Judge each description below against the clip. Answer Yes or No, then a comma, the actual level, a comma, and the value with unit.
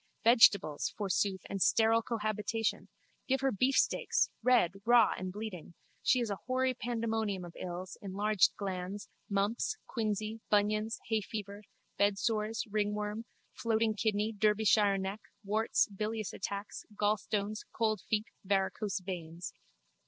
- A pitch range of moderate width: No, narrow, 2.0 semitones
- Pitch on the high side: Yes, high, 210 Hz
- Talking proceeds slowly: Yes, slow, 115 wpm